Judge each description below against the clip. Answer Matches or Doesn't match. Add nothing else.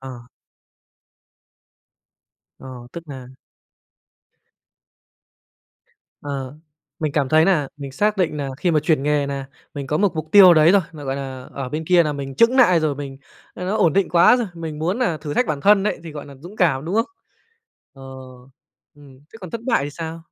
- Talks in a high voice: Doesn't match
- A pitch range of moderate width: Matches